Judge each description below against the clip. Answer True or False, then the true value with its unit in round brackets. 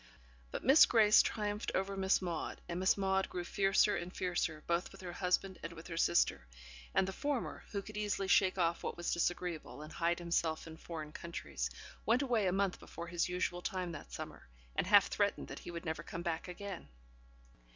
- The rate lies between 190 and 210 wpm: True (200 wpm)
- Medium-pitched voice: True (180 Hz)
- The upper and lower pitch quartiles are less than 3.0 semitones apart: True (2.5 semitones)